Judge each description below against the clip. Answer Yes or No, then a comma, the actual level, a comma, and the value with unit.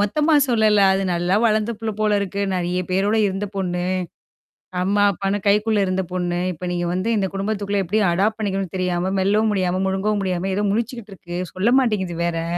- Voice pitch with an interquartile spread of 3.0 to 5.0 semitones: No, narrow, 2.6 semitones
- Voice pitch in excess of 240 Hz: No, high, 195 Hz